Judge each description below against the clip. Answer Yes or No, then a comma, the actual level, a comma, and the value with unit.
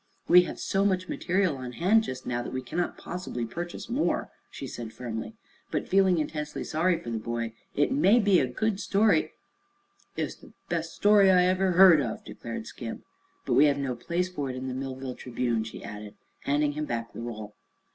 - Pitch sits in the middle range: Yes, medium, 150 Hz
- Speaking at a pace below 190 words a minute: No, average, 200 wpm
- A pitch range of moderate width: No, wide, 7.0 semitones